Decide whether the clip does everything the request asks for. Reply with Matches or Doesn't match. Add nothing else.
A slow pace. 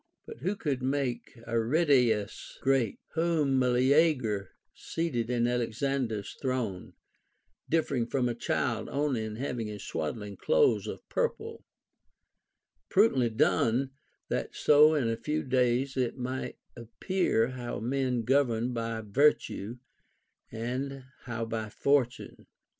Matches